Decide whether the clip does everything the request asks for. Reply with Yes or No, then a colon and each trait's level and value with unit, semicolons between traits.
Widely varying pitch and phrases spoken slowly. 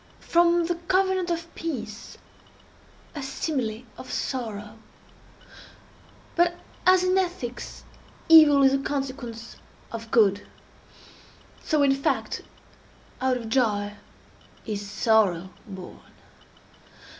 Yes: wide, 7.1 semitones; slow, 100 wpm